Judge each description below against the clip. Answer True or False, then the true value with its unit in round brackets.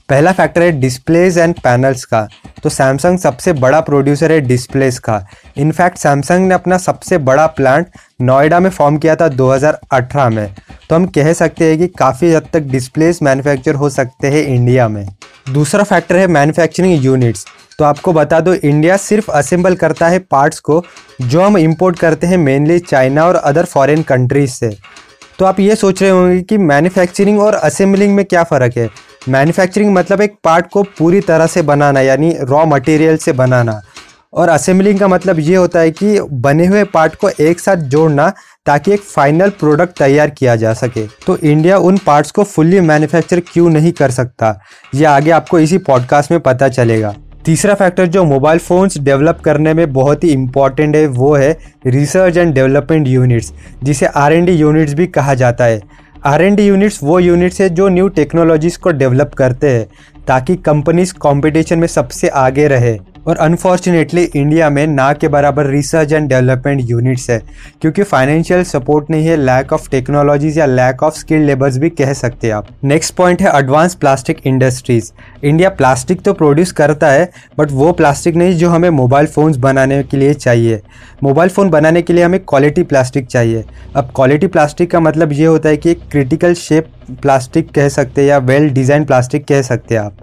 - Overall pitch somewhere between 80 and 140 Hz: False (150 Hz)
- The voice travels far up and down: False (4.4 semitones)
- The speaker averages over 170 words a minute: True (185 wpm)